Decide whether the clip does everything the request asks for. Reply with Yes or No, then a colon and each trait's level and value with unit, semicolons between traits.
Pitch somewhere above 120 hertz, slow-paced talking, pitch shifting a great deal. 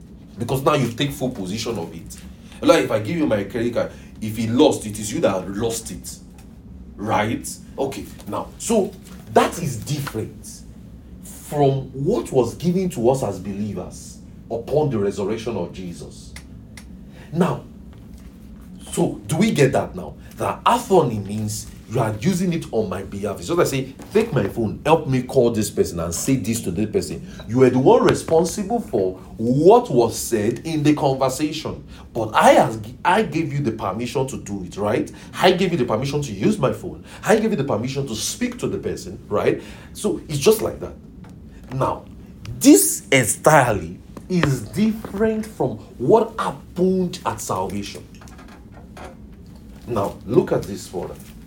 No: low, 135 Hz; average, 170 wpm; wide, 8.5 semitones